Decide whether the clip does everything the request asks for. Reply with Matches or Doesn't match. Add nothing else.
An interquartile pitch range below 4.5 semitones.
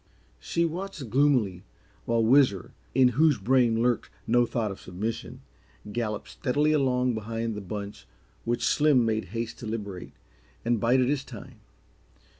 Matches